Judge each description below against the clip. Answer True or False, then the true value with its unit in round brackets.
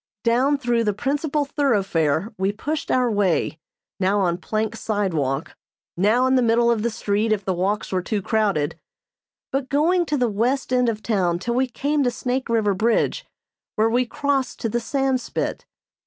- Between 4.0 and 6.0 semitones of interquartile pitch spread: True (4.3 semitones)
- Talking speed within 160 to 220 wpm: True (175 wpm)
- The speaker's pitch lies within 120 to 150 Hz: False (230 Hz)